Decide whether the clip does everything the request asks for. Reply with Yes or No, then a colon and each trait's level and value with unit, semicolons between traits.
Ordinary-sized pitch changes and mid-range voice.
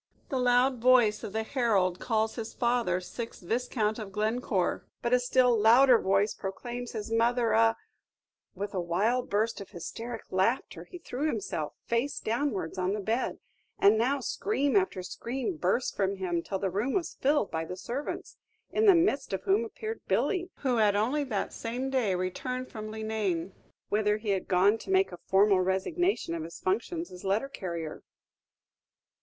No: average, 4.5 semitones; high, 220 Hz